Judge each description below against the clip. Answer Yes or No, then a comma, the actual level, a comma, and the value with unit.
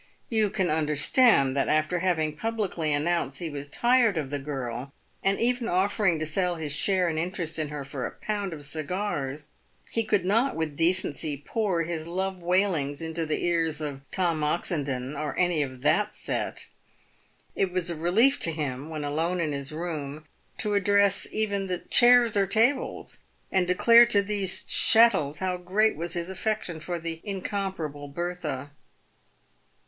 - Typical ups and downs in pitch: Yes, average, 4.7 semitones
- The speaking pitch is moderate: Yes, medium, 170 Hz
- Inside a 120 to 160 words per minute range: No, average, 170 wpm